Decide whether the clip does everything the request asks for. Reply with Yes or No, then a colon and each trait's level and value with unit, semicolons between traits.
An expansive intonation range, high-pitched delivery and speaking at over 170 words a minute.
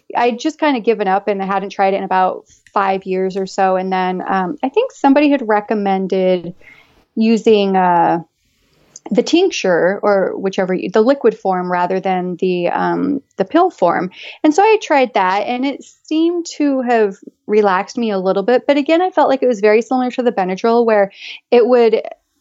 Yes: wide, 6.0 semitones; high, 215 Hz; average, 190 wpm